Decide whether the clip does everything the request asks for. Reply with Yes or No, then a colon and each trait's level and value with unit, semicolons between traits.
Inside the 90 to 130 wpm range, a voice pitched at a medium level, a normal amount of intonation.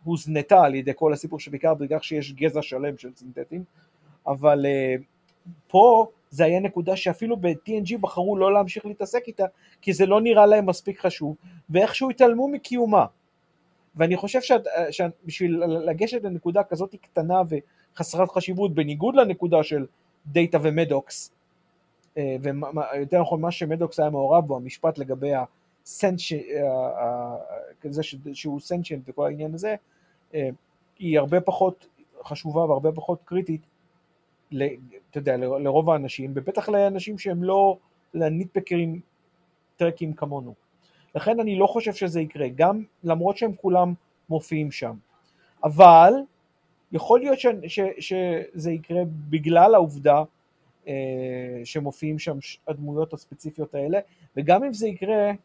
Yes: average, 120 wpm; medium, 170 Hz; average, 4.0 semitones